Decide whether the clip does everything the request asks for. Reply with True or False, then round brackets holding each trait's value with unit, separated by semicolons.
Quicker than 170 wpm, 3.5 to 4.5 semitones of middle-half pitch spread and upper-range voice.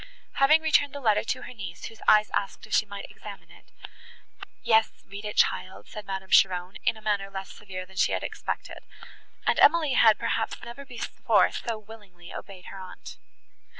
False (185 wpm; 3.1 semitones; 210 Hz)